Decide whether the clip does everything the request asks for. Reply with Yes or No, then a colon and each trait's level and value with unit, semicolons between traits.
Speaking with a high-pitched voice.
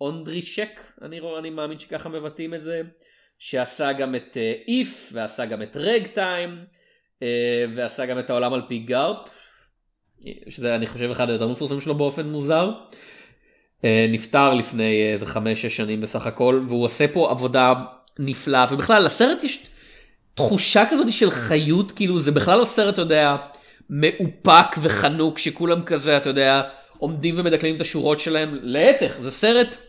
No: medium, 150 Hz